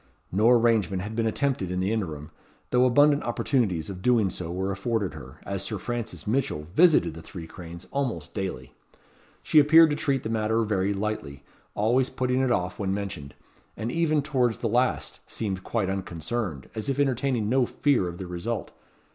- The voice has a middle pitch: No, low, 110 Hz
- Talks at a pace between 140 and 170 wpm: No, average, 180 wpm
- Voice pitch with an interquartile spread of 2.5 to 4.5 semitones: No, average, 5.2 semitones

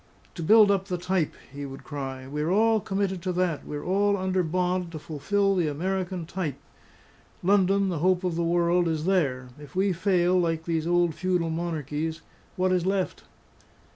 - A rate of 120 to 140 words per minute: No, average, 175 wpm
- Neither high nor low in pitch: Yes, medium, 175 Hz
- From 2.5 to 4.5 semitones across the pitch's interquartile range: Yes, average, 2.8 semitones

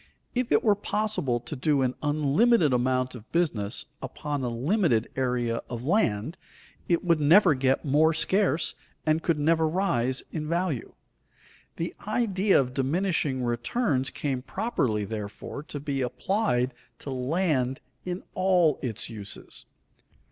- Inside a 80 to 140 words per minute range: Yes, slow, 135 wpm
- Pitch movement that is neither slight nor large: No, wide, 5.8 semitones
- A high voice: No, medium, 145 Hz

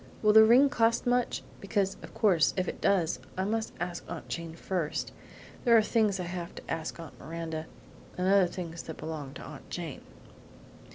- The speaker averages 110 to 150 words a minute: No, average, 180 wpm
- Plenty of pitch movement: No, average, 4.6 semitones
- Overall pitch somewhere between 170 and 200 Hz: Yes, medium, 185 Hz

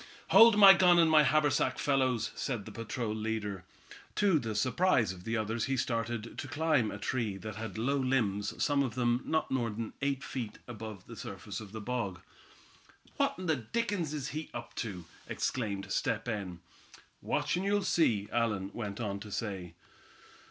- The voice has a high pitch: No, low, 120 Hz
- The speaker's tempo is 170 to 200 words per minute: Yes, average, 180 wpm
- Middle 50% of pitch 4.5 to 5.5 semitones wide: Yes, average, 5.1 semitones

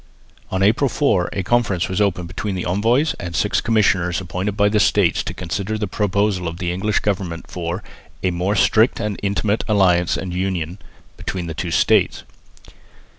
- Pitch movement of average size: Yes, average, 3.0 semitones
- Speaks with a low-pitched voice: Yes, very low, 95 Hz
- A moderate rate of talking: Yes, average, 175 wpm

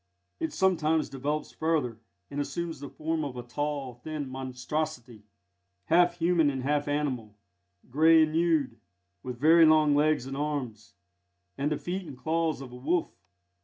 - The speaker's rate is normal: Yes, average, 155 wpm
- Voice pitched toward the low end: No, medium, 150 Hz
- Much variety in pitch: No, average, 3.6 semitones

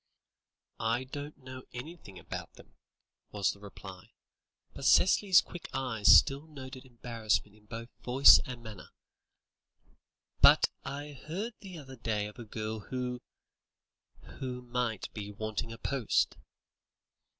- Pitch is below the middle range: Yes, low, 125 Hz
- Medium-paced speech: No, slow, 130 wpm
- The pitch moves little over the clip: No, average, 4.0 semitones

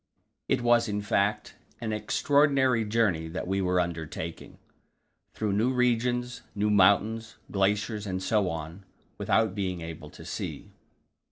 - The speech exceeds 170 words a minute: No, slow, 135 wpm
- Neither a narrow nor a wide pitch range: Yes, average, 3.7 semitones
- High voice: No, low, 105 Hz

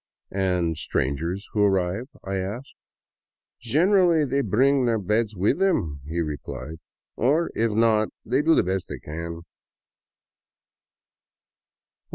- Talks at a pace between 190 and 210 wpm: No, slow, 135 wpm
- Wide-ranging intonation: Yes, wide, 6.7 semitones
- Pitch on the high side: No, low, 105 Hz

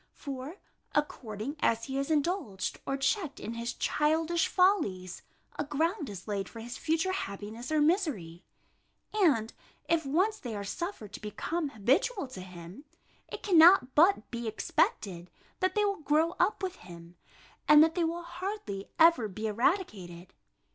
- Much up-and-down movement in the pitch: Yes, wide, 8.5 semitones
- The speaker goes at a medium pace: Yes, average, 155 wpm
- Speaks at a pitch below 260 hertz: No, very high, 280 Hz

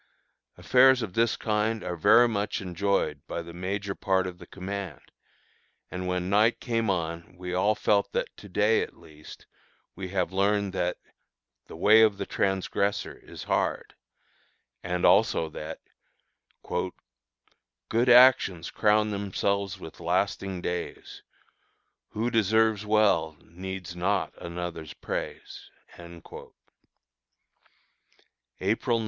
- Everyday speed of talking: No, slow, 120 wpm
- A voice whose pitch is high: No, very low, 95 Hz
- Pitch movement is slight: No, average, 3.2 semitones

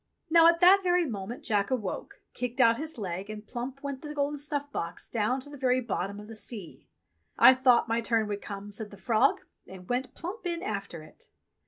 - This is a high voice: Yes, high, 240 Hz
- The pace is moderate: No, fast, 210 wpm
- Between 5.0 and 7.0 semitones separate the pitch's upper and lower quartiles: Yes, wide, 5.6 semitones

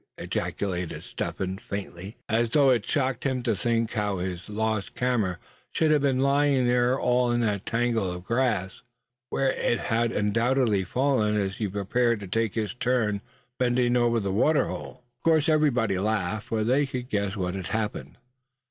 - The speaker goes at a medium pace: Yes, average, 175 wpm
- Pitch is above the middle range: No, low, 115 Hz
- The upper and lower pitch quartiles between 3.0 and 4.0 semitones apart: Yes, average, 3.7 semitones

